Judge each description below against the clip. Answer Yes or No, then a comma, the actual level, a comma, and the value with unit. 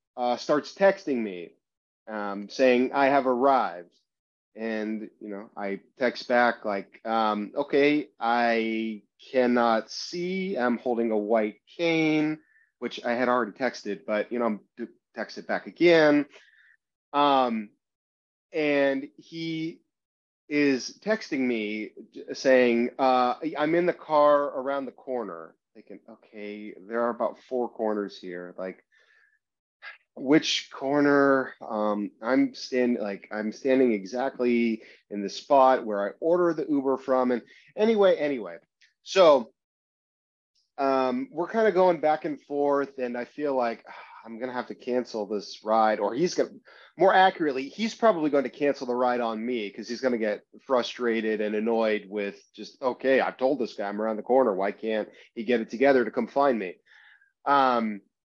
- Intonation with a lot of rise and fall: No, average, 4.7 semitones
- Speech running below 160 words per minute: Yes, average, 150 wpm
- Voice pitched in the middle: No, low, 125 Hz